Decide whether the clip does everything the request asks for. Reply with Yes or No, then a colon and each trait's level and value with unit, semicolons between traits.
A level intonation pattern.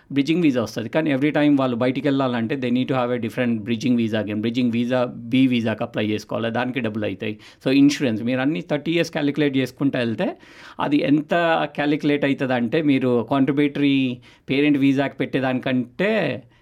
No: average, 3.3 semitones